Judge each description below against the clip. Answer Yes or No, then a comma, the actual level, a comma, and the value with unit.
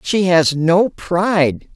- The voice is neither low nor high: Yes, medium, 175 Hz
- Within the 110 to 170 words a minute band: Yes, slow, 135 wpm